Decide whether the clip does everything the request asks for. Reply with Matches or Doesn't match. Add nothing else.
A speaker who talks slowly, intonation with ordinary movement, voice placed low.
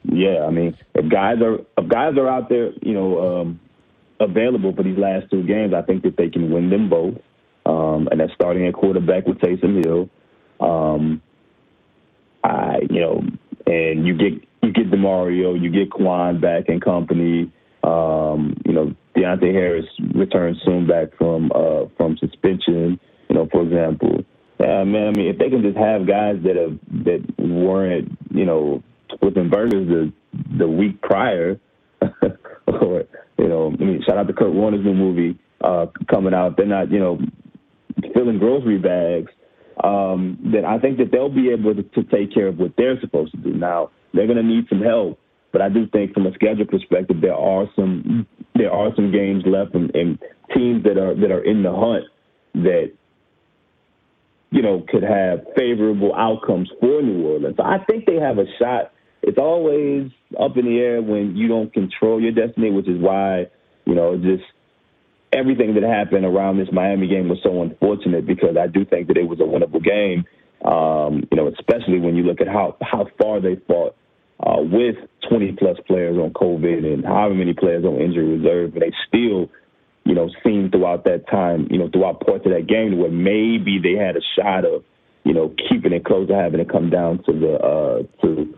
Doesn't match